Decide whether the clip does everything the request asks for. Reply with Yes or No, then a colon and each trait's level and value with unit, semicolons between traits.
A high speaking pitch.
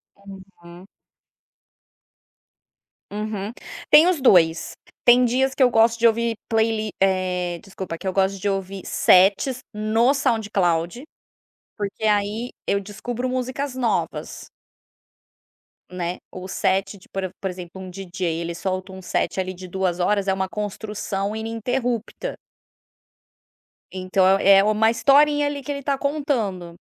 Yes: high, 205 Hz